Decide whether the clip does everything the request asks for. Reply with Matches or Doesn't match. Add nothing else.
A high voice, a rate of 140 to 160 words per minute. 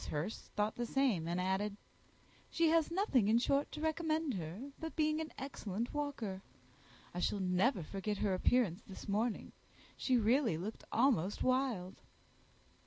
Matches